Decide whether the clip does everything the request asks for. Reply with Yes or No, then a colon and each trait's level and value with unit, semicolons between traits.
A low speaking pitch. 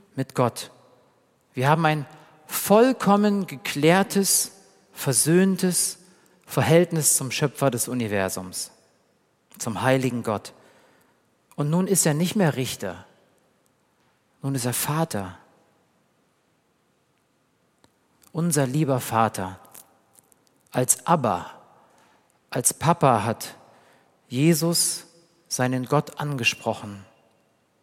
No: medium, 145 Hz